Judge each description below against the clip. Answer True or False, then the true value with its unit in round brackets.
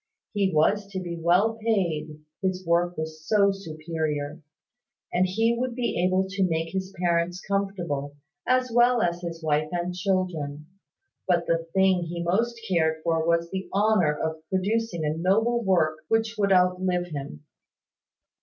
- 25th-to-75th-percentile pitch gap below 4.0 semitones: True (3.4 semitones)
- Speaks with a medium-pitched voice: True (180 Hz)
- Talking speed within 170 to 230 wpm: False (155 wpm)